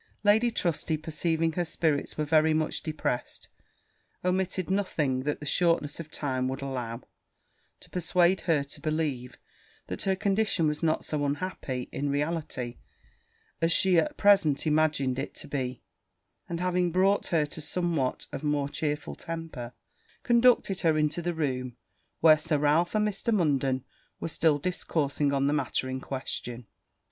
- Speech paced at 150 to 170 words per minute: Yes, average, 155 wpm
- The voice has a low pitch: No, medium, 155 Hz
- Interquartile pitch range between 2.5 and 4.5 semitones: Yes, average, 3.7 semitones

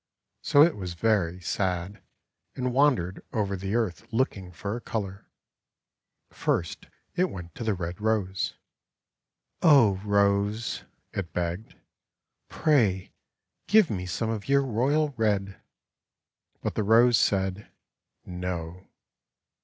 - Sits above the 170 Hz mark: No, low, 100 Hz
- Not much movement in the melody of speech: No, average, 4.1 semitones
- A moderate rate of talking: No, slow, 120 wpm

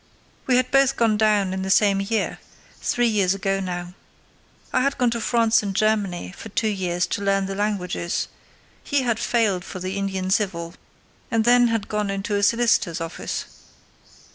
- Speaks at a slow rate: No, average, 170 wpm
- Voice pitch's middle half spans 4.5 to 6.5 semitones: No, average, 3.2 semitones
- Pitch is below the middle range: No, high, 200 Hz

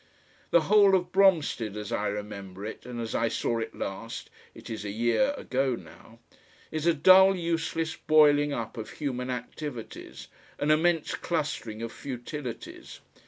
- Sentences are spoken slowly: No, average, 155 wpm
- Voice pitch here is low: Yes, low, 130 Hz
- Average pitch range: No, wide, 6.4 semitones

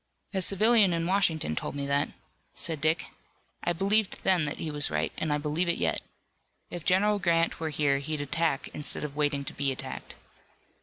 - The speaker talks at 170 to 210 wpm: Yes, average, 190 wpm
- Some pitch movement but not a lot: Yes, average, 4.0 semitones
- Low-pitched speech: No, medium, 160 Hz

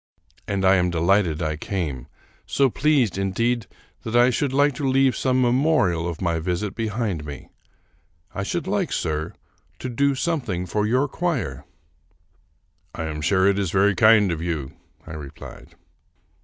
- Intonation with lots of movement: Yes, wide, 7.0 semitones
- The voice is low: Yes, low, 100 Hz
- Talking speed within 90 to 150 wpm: No, average, 160 wpm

